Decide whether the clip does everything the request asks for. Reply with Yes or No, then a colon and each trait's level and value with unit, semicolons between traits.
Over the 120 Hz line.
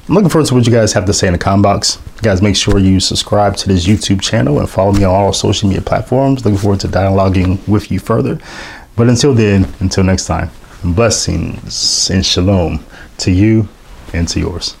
No: low, 100 Hz